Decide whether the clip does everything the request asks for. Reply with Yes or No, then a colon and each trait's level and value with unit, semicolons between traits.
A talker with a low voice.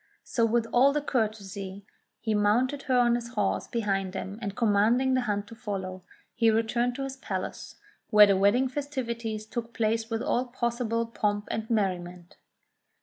No: high, 225 Hz